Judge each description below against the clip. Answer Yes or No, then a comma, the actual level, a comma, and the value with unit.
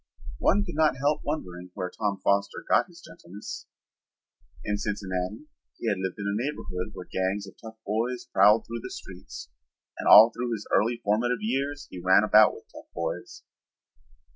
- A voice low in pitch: Yes, low, 105 Hz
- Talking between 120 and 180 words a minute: Yes, average, 170 wpm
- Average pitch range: Yes, average, 4.0 semitones